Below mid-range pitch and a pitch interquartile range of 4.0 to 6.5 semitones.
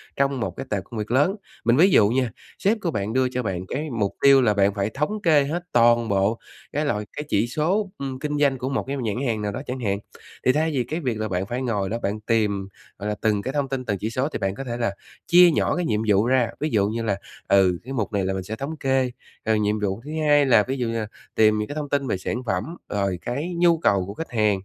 Yes: low, 120 Hz; average, 5.0 semitones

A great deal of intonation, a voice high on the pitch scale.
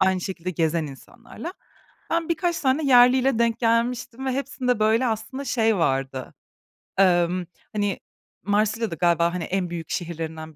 Yes: wide, 6.5 semitones; high, 215 Hz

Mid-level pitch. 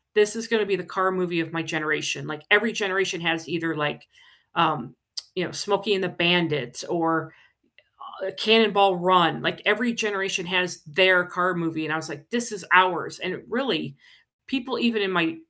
Yes: medium, 180 Hz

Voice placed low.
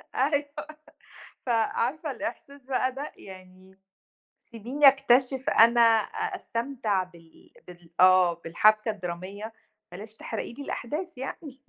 No: high, 235 Hz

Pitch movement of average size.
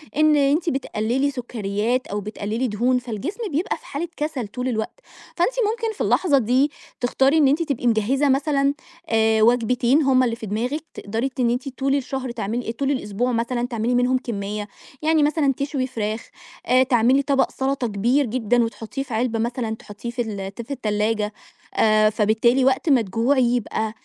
Yes: average, 3.7 semitones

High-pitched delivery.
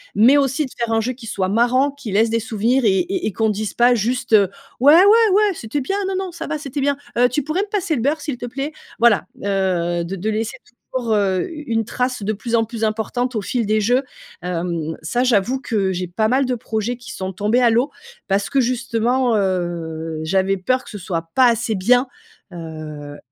Yes: high, 230 Hz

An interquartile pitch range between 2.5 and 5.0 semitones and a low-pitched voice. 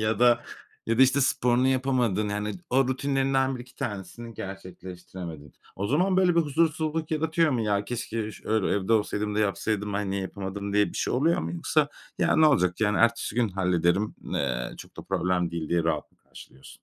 No: wide, 5.6 semitones; low, 110 Hz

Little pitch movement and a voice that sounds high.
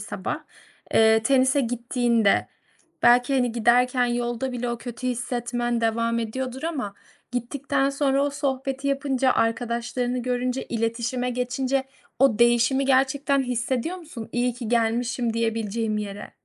Yes: narrow, 2.2 semitones; high, 245 Hz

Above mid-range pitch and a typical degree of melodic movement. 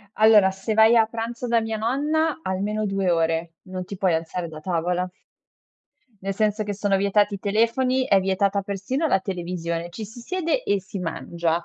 Yes: high, 200 Hz; average, 3.6 semitones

